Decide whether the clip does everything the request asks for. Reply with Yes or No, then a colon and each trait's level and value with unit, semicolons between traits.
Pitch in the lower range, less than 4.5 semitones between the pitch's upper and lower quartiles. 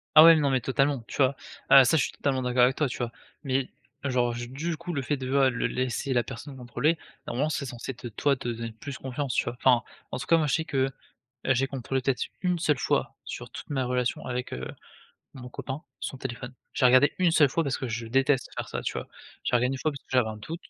Yes: low, 130 Hz; narrow, 2.4 semitones